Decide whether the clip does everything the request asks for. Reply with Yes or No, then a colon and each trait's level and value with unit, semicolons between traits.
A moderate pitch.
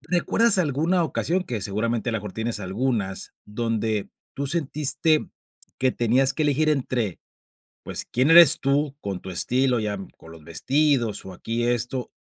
No: low, 125 Hz